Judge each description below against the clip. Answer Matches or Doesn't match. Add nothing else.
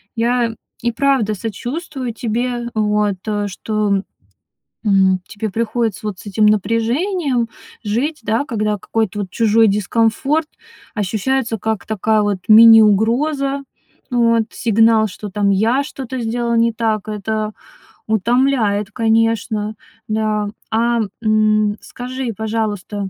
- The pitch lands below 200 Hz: Doesn't match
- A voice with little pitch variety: Matches